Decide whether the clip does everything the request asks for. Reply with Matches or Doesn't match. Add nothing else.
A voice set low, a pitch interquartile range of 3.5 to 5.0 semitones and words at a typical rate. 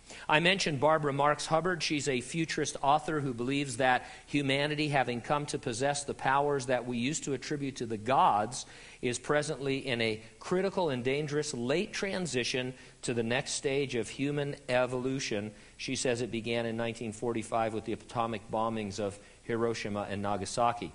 Matches